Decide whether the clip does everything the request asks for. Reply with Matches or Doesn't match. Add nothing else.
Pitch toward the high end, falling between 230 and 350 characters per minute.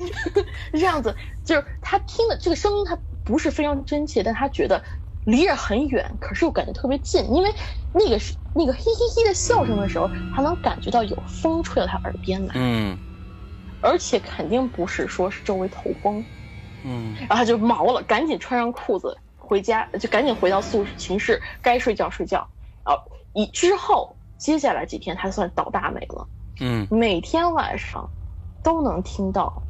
Matches